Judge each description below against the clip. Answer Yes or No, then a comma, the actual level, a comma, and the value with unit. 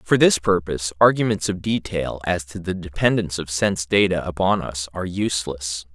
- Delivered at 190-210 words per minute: No, average, 170 wpm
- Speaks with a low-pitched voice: Yes, very low, 90 Hz